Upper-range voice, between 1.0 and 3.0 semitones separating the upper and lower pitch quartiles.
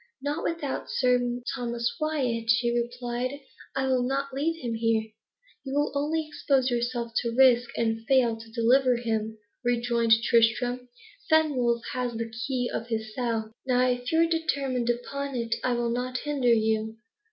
Yes: high, 245 Hz; narrow, 2.4 semitones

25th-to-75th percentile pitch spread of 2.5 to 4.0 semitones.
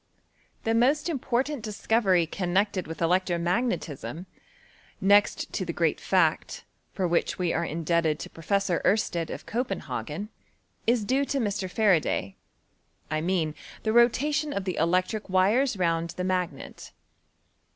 No: average, 4.9 semitones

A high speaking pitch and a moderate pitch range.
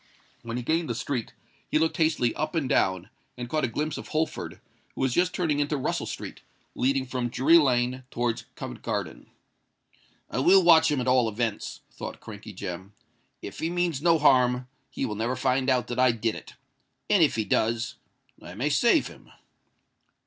No: low, 130 Hz; average, 4.7 semitones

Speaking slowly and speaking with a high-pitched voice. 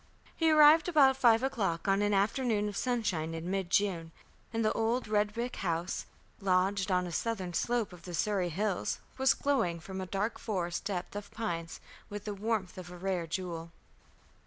No: average, 185 wpm; high, 200 Hz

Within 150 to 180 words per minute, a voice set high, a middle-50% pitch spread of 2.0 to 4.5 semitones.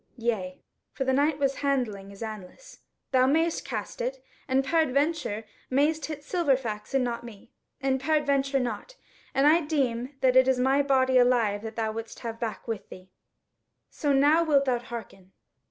Yes: average, 170 wpm; very high, 260 Hz; average, 4.0 semitones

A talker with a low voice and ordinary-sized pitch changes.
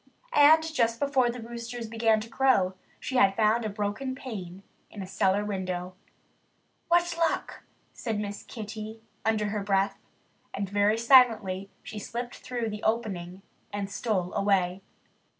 No: high, 215 Hz; average, 3.3 semitones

